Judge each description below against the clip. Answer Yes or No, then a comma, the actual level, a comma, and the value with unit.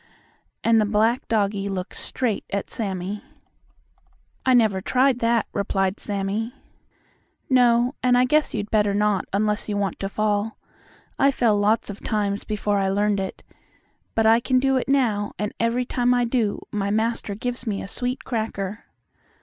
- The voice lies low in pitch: No, high, 215 Hz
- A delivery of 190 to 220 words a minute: No, average, 165 wpm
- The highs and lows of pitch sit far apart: No, average, 3.1 semitones